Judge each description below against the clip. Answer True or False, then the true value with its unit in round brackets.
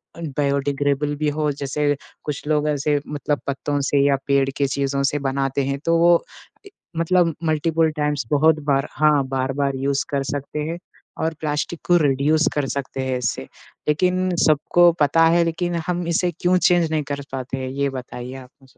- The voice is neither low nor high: True (145 Hz)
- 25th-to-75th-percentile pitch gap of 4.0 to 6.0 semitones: False (2.7 semitones)